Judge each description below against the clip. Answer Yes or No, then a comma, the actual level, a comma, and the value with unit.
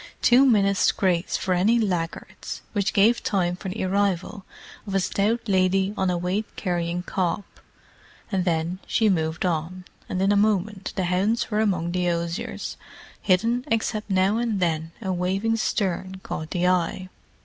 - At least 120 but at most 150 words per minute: No, average, 160 wpm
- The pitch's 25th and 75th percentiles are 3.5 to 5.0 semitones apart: No, narrow, 2.6 semitones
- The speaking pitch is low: No, high, 190 Hz